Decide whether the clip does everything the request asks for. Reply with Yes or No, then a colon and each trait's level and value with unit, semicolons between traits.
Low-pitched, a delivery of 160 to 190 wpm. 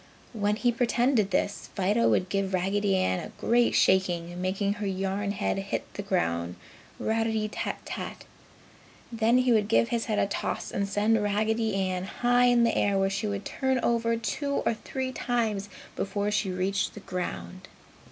No: high, 205 Hz; average, 170 wpm